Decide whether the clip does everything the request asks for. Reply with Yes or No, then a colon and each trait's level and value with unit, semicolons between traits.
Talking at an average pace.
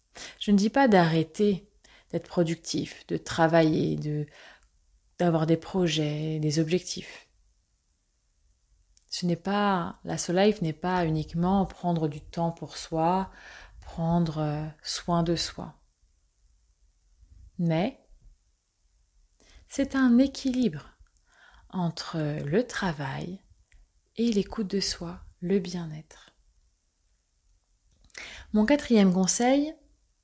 No: slow, 95 wpm